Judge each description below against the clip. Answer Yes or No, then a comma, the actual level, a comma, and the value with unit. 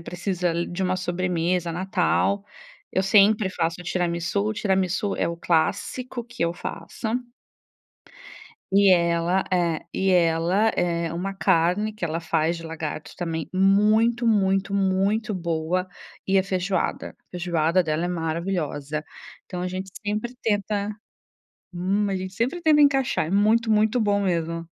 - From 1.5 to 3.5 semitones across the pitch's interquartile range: Yes, average, 3.2 semitones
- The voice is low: No, medium, 185 Hz